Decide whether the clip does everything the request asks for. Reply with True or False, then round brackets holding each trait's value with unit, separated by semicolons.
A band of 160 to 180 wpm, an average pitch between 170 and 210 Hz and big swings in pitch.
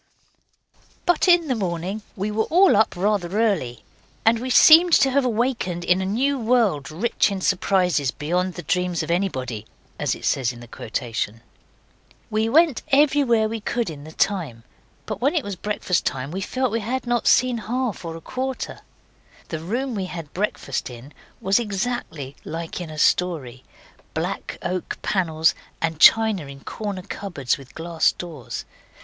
True (165 wpm; 190 Hz; 6.5 semitones)